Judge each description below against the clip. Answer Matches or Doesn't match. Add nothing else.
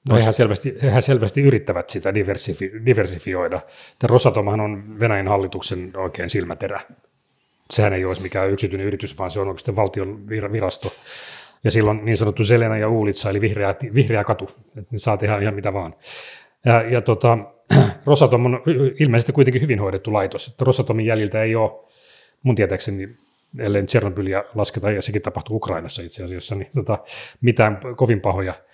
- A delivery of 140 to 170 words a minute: Matches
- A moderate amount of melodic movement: Matches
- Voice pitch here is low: Matches